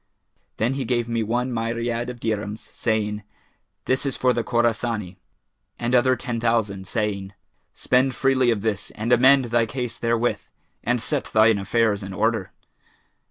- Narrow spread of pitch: Yes, narrow, 2.2 semitones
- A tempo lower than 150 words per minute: No, average, 155 wpm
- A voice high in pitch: No, low, 115 Hz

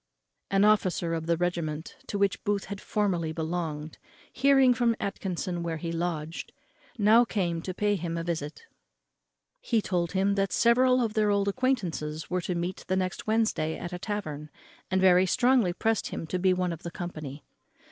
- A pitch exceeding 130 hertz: Yes, medium, 185 Hz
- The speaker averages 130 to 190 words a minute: Yes, average, 180 wpm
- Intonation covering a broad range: No, average, 3.7 semitones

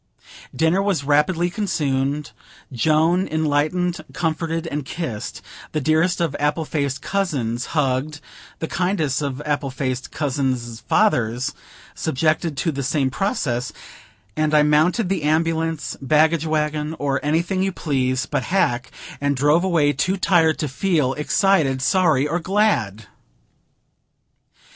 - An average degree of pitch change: Yes, average, 3.6 semitones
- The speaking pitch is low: No, medium, 150 Hz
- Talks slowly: Yes, slow, 125 wpm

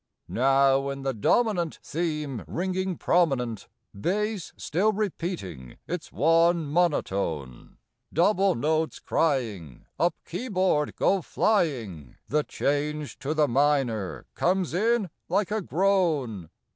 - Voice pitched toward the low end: No, medium, 155 Hz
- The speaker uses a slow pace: Yes, slow, 105 wpm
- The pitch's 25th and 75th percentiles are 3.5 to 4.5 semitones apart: No, wide, 5.5 semitones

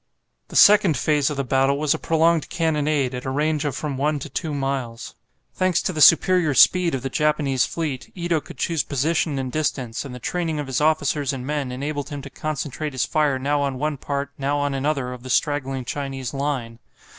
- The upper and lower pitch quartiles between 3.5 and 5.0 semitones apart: No, narrow, 2.4 semitones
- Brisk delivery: Yes, fast, 210 wpm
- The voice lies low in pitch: No, medium, 145 Hz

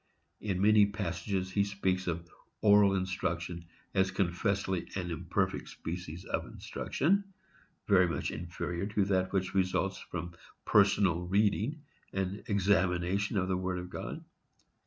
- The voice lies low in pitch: Yes, very low, 95 Hz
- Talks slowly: Yes, slow, 130 wpm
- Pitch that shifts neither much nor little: No, narrow, 2.1 semitones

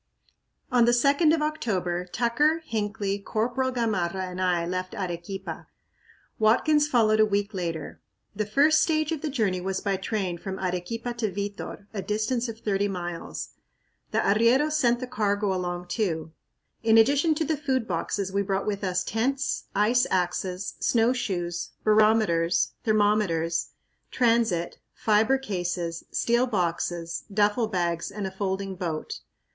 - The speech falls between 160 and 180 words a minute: No, average, 140 wpm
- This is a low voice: No, high, 205 Hz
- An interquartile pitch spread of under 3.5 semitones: No, average, 4.6 semitones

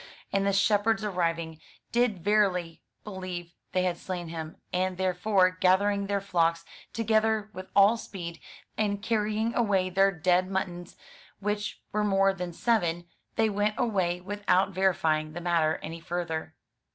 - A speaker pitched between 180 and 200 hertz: Yes, high, 190 Hz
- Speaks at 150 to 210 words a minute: No, average, 140 wpm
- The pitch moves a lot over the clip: No, average, 2.9 semitones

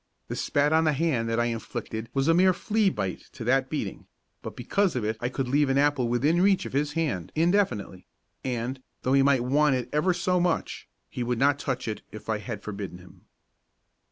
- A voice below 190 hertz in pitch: Yes, low, 135 Hz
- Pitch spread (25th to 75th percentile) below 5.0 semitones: No, average, 5.3 semitones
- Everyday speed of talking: No, fast, 210 wpm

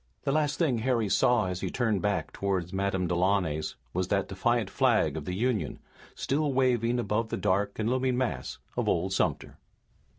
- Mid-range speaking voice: No, low, 105 Hz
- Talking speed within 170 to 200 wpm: Yes, average, 175 wpm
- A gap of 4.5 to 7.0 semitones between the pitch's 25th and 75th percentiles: Yes, average, 4.8 semitones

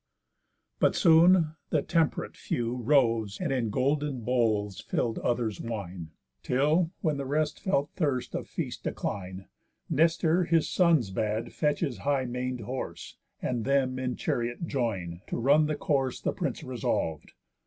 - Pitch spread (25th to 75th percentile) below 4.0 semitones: No, average, 4.8 semitones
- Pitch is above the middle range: No, low, 130 Hz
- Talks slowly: No, average, 145 wpm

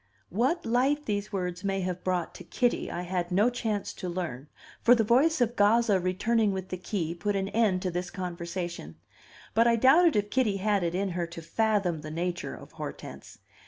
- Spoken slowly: No, average, 195 wpm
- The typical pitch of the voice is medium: No, high, 195 Hz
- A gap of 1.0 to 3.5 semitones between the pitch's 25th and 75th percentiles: No, average, 4.2 semitones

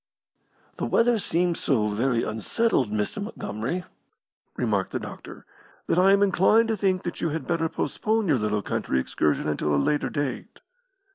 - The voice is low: No, medium, 160 Hz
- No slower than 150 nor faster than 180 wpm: Yes, average, 160 wpm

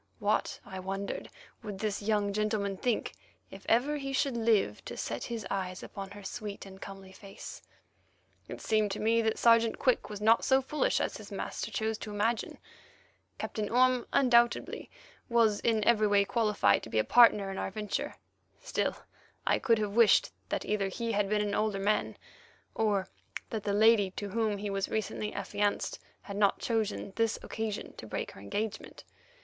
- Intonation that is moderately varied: No, narrow, 2.3 semitones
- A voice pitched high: Yes, high, 210 Hz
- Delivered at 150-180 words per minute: Yes, average, 175 wpm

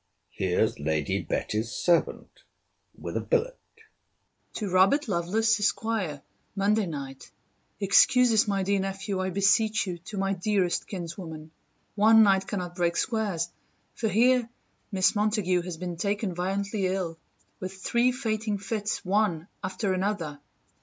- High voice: Yes, high, 195 Hz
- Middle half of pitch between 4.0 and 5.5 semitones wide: No, average, 3.4 semitones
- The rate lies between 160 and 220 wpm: No, slow, 135 wpm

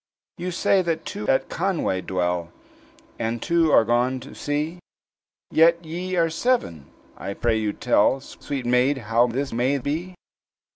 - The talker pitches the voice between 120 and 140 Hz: Yes, low, 135 Hz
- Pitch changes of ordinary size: No, wide, 6.6 semitones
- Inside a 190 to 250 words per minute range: No, average, 150 wpm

